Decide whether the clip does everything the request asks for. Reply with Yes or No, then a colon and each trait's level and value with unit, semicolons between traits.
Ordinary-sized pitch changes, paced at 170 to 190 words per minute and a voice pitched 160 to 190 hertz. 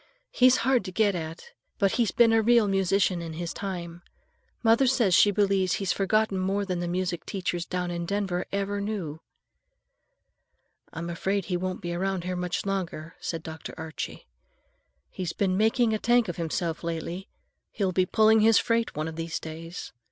Yes: average, 3.2 semitones; average, 175 wpm; medium, 185 Hz